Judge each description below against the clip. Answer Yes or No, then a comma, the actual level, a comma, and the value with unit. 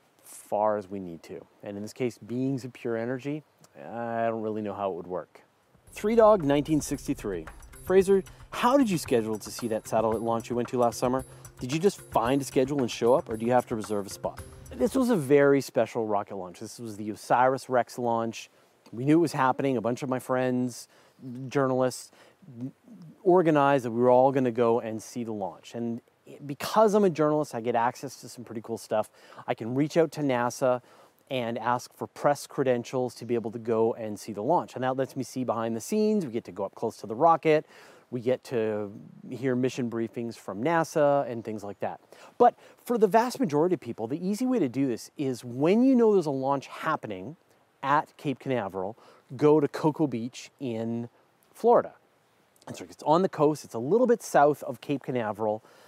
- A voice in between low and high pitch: No, low, 125 Hz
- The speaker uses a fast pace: Yes, fast, 210 wpm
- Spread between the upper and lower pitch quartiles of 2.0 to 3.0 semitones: No, average, 4.2 semitones